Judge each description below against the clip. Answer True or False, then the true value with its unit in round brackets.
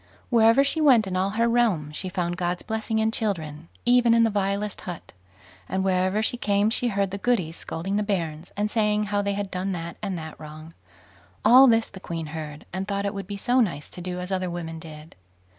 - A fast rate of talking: True (220 wpm)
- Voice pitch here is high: True (195 Hz)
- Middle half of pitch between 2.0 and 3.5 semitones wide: False (4.0 semitones)